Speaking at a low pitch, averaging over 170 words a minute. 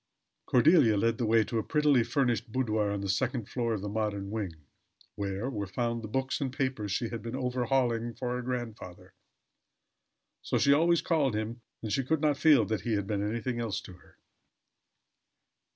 Yes: low, 115 Hz; average, 185 wpm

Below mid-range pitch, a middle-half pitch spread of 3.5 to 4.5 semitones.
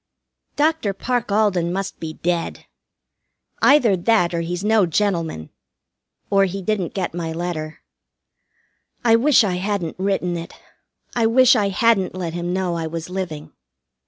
No: medium, 185 Hz; average, 3.8 semitones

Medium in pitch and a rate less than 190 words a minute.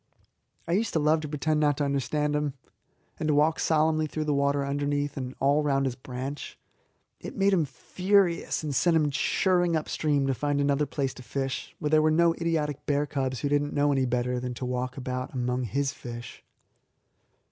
No: medium, 145 Hz; average, 200 wpm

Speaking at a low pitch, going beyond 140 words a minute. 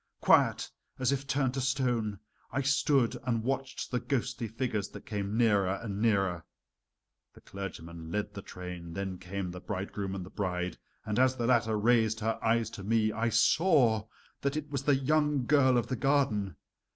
Yes: low, 115 Hz; average, 175 wpm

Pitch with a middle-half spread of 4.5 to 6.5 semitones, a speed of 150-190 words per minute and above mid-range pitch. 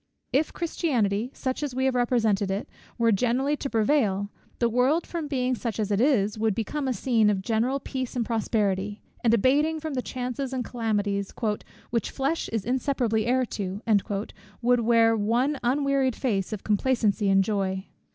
No: average, 3.9 semitones; average, 165 wpm; high, 235 Hz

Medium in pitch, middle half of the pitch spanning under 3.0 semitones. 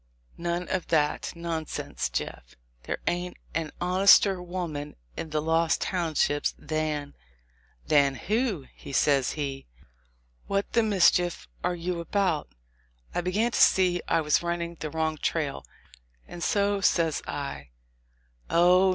No: medium, 170 Hz; average, 3.3 semitones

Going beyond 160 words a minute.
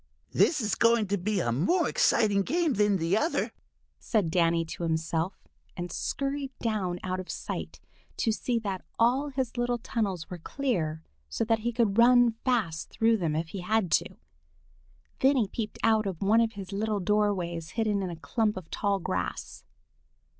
Yes: average, 175 wpm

